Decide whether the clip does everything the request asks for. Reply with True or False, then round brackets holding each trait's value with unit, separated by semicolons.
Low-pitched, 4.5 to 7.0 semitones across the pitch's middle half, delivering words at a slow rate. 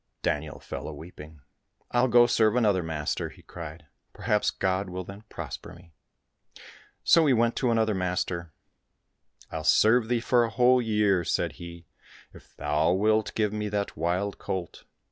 False (100 Hz; 4.8 semitones; 175 wpm)